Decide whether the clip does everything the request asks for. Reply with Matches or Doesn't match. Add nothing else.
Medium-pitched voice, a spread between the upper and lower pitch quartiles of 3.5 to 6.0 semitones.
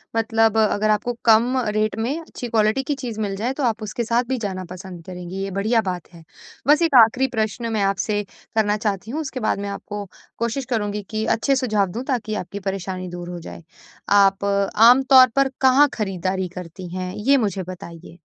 Doesn't match